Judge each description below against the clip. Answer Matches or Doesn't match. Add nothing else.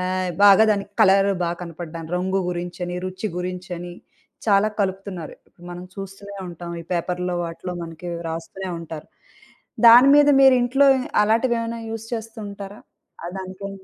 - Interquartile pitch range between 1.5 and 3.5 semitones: Matches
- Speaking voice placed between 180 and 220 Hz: Matches